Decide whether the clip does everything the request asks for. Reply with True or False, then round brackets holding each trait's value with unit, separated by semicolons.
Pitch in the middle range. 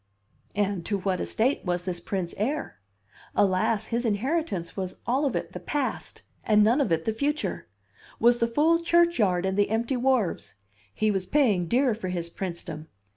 False (210 Hz)